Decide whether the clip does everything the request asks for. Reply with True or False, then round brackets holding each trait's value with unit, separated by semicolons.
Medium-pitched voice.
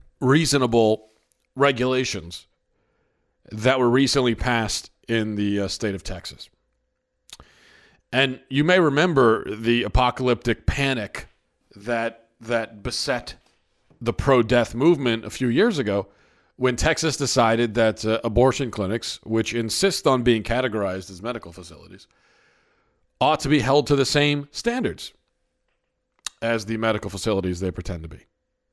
False (115 Hz)